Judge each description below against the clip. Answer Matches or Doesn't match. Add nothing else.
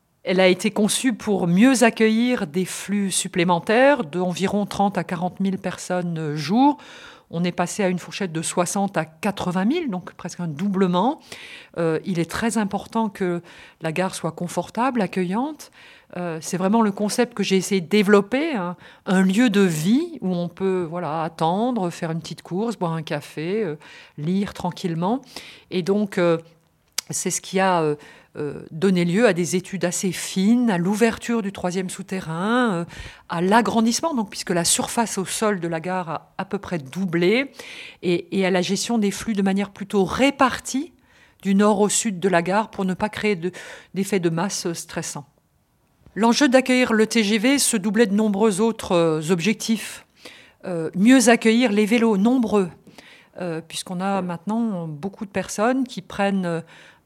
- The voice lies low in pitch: Doesn't match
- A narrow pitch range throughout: Doesn't match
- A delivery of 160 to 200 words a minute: Matches